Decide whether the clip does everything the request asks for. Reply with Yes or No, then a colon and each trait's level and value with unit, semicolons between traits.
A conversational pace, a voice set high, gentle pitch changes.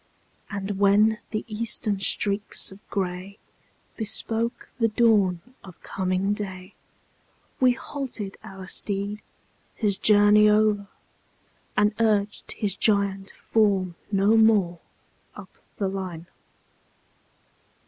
No: slow, 100 wpm; high, 205 Hz; narrow, 1.9 semitones